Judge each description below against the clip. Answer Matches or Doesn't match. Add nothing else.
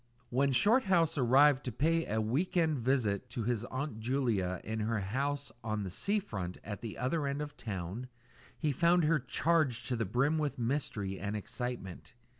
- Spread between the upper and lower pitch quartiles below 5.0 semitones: Doesn't match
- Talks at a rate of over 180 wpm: Matches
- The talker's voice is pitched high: Doesn't match